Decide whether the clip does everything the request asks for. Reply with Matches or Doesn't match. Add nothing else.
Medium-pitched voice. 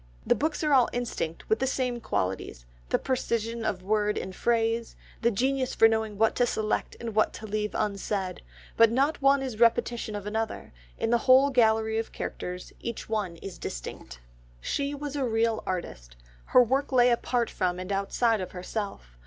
Doesn't match